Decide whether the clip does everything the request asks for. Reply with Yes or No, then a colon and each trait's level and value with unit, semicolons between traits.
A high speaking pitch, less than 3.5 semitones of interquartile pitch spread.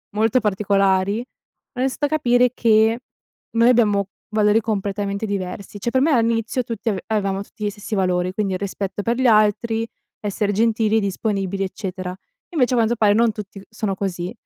Yes: high, 210 Hz; narrow, 2.6 semitones